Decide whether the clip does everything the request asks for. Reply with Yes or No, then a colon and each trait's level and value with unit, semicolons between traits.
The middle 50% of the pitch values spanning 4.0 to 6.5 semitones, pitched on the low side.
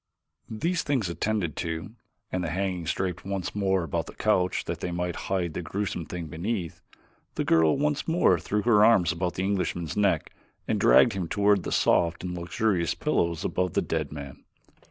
No: average, 3.3 semitones; very low, 90 Hz